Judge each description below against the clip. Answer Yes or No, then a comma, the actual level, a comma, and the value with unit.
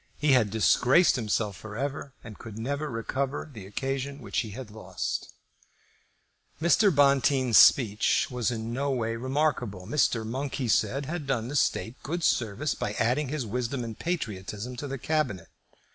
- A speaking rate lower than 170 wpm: Yes, average, 160 wpm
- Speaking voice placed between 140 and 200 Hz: No, low, 125 Hz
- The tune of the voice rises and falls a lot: No, average, 4.1 semitones